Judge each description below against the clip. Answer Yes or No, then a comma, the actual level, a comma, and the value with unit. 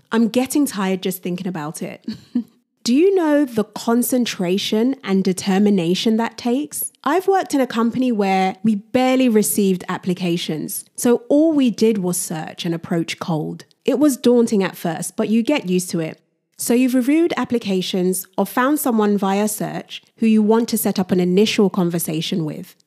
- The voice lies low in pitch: No, high, 210 Hz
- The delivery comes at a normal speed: Yes, average, 170 wpm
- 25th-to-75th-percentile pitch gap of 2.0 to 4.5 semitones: No, average, 4.9 semitones